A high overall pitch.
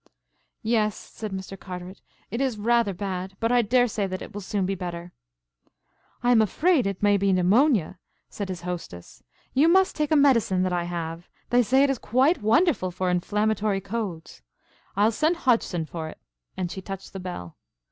Yes: high, 200 Hz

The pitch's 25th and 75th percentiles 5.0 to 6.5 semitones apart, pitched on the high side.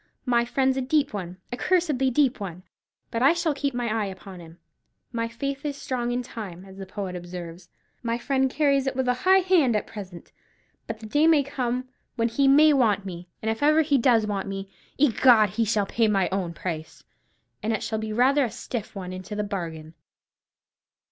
Yes: wide, 5.6 semitones; high, 230 Hz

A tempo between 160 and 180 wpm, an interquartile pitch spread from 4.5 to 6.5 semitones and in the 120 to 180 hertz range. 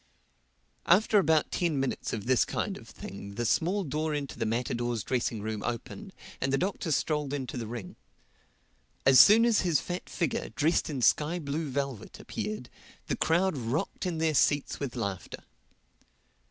Yes: average, 165 wpm; wide, 5.4 semitones; medium, 140 Hz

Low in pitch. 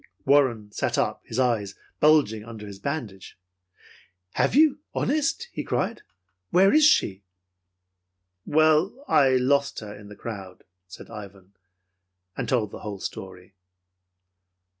Yes: low, 115 Hz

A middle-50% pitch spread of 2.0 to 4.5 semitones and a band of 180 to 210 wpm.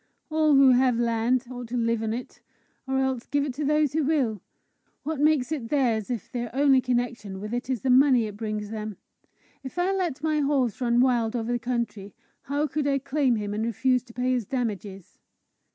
Yes: average, 3.4 semitones; fast, 205 wpm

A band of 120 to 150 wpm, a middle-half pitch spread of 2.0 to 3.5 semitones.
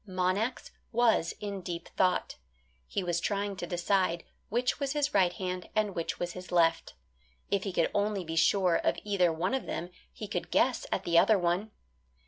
No: average, 185 wpm; average, 2.9 semitones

